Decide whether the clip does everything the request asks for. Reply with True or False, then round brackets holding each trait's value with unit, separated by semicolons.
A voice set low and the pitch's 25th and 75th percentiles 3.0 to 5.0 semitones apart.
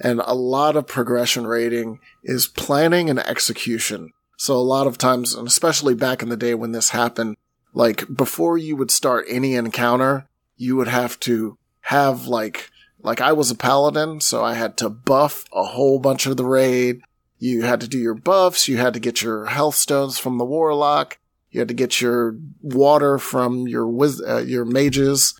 False (125 Hz; 2.6 semitones)